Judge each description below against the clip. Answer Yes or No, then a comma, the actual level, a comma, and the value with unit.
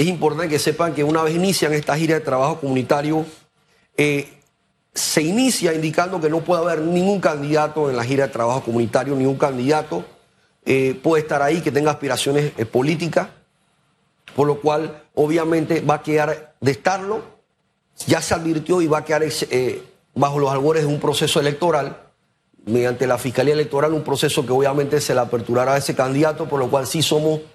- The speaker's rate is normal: Yes, average, 180 wpm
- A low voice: No, medium, 150 Hz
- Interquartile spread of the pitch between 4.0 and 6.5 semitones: No, narrow, 2.6 semitones